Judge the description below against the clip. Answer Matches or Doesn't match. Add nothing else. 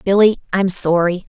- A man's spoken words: Doesn't match